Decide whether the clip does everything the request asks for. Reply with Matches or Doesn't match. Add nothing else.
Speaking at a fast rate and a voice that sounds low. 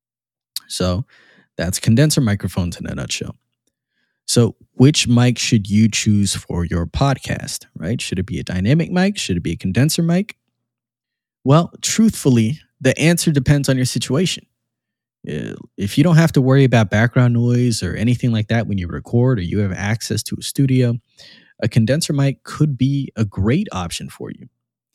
Doesn't match